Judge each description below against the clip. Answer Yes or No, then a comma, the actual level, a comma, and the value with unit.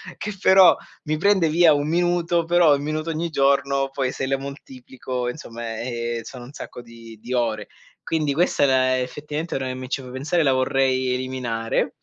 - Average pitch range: Yes, average, 3.6 semitones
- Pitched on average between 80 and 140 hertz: Yes, low, 135 Hz